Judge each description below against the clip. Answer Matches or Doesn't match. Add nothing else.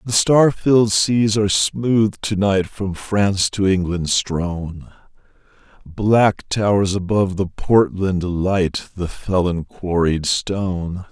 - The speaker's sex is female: Doesn't match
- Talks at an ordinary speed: Doesn't match